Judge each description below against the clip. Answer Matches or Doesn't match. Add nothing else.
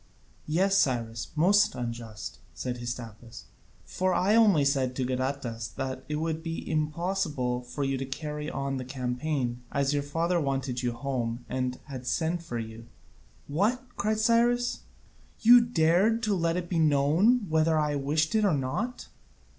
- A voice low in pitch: Doesn't match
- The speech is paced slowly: Doesn't match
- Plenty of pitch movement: Matches